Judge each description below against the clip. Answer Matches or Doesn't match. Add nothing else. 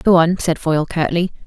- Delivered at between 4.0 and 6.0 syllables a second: Matches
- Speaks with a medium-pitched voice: Matches